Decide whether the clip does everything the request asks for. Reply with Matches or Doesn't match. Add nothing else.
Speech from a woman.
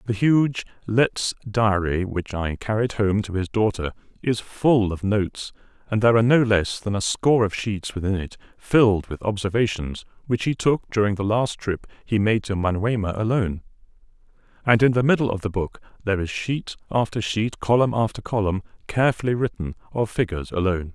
Doesn't match